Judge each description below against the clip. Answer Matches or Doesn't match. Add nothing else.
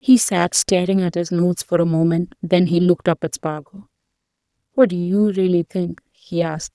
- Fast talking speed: Doesn't match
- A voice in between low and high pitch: Matches